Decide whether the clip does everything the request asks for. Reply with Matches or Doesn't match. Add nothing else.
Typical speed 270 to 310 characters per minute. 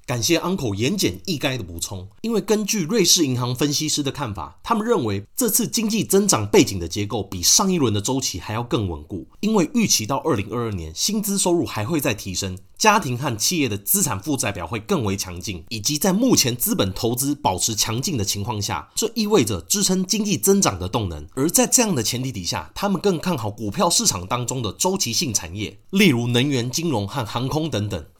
Doesn't match